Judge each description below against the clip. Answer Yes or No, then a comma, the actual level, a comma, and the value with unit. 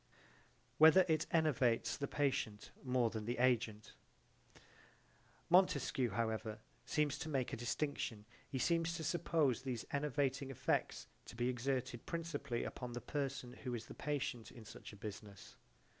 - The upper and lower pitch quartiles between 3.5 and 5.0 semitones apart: Yes, average, 4.0 semitones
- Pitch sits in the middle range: No, low, 130 Hz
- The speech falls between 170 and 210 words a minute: No, average, 145 wpm